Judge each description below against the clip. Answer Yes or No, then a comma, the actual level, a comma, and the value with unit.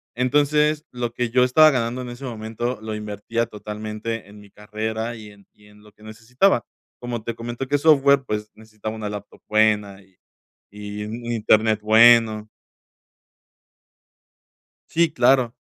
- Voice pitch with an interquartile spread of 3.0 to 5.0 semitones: No, narrow, 2.6 semitones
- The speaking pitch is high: No, low, 110 Hz